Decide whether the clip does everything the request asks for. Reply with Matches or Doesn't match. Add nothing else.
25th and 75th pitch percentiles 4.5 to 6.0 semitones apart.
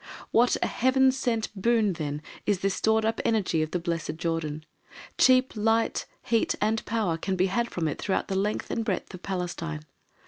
Matches